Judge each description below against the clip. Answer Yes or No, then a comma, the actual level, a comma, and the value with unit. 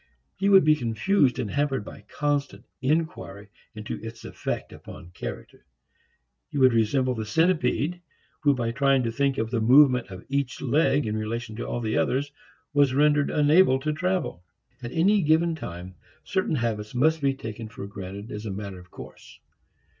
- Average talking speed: Yes, average, 170 wpm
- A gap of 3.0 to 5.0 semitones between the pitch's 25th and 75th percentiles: No, wide, 5.4 semitones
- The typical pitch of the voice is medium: No, low, 130 Hz